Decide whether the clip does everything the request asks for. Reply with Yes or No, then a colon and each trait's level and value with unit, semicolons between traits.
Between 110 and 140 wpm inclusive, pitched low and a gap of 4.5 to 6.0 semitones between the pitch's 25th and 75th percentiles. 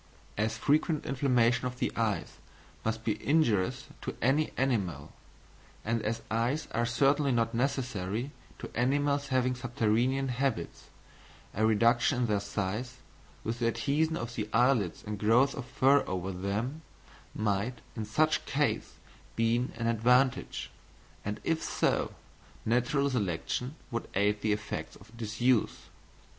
No: slow, 135 wpm; low, 120 Hz; average, 3.7 semitones